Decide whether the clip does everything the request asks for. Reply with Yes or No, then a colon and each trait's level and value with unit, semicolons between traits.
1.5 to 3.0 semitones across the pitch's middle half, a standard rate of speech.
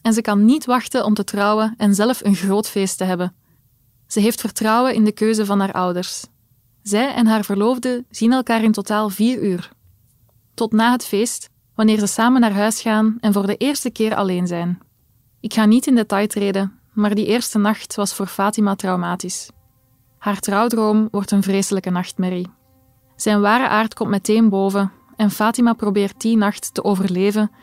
Yes: narrow, 2.4 semitones; average, 180 wpm